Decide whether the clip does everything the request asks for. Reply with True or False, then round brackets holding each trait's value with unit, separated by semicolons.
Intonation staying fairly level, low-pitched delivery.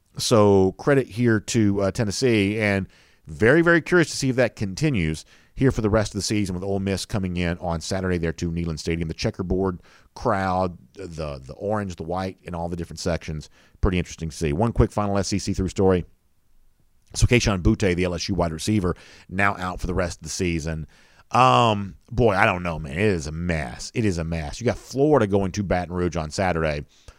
False (4.1 semitones; 95 Hz)